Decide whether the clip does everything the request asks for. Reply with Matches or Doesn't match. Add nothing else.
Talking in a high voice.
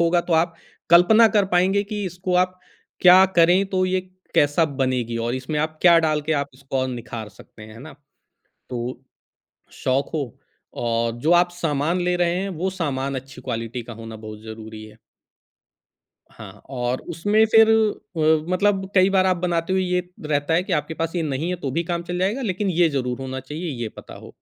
Doesn't match